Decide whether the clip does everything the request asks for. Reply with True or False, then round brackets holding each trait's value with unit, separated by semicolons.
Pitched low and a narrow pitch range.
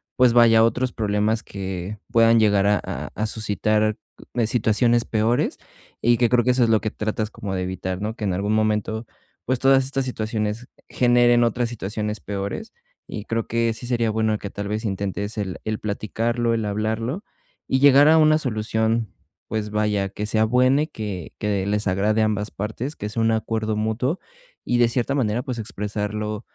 True (110 Hz; 2.2 semitones)